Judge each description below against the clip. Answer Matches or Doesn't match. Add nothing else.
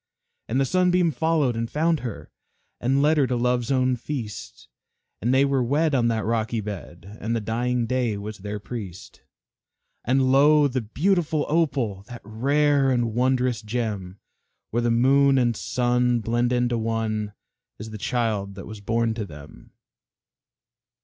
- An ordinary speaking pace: Matches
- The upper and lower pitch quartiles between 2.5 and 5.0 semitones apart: Matches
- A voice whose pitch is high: Doesn't match